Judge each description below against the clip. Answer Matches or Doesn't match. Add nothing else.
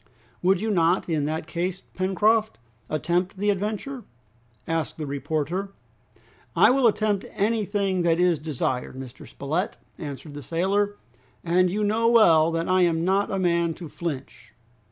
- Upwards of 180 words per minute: Doesn't match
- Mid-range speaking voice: Matches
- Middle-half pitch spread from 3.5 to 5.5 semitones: Matches